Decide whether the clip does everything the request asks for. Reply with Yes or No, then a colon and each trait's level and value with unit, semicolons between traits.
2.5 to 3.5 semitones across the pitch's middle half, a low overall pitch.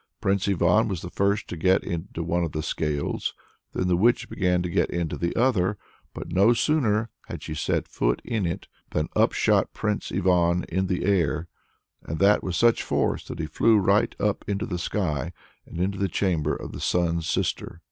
Yes: average, 3.0 semitones; very low, 90 Hz